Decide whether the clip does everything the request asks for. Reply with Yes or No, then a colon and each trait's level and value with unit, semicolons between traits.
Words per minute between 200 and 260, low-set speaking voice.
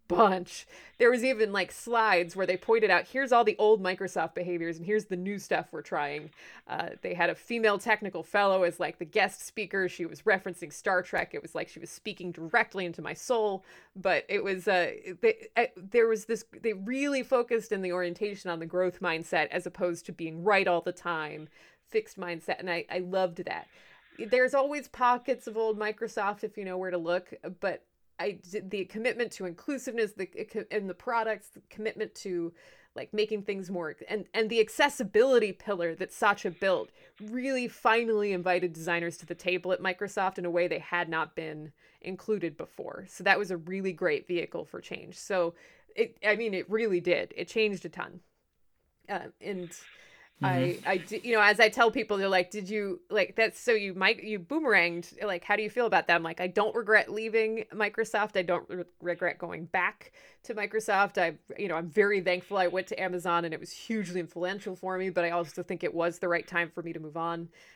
No: fast, 205 wpm; high, 195 Hz